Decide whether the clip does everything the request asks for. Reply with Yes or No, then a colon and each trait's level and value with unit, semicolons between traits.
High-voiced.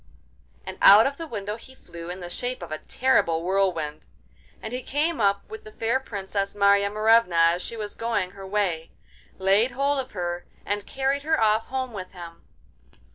Yes: high, 205 Hz